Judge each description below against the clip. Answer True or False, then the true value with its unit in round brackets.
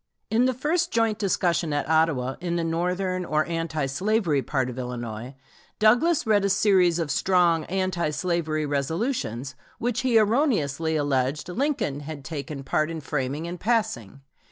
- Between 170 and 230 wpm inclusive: False (155 wpm)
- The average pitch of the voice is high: False (165 Hz)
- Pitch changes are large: True (6.1 semitones)